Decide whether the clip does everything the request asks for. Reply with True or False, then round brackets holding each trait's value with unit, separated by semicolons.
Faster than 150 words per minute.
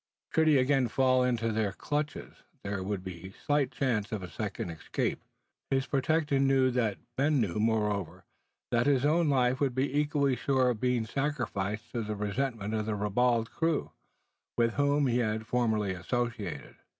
True (170 wpm)